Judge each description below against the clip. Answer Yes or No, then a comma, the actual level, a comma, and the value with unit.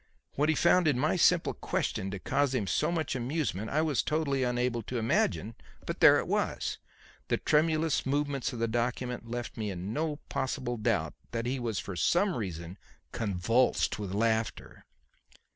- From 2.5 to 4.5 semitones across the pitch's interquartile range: No, average, 5.1 semitones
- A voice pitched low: Yes, low, 125 Hz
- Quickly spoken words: No, average, 170 wpm